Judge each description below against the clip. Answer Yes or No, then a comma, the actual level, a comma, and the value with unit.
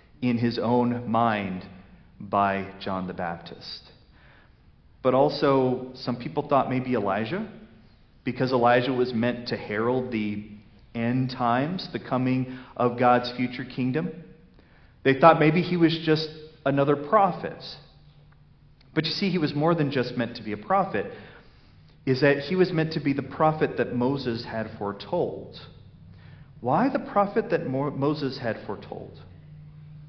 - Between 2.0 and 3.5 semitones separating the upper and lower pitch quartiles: No, average, 4.0 semitones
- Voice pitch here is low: Yes, low, 130 Hz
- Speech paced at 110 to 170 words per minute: Yes, average, 140 wpm